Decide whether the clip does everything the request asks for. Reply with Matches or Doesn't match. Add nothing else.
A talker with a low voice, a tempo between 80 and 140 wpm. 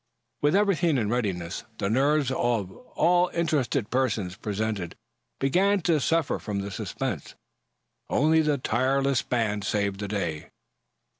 Matches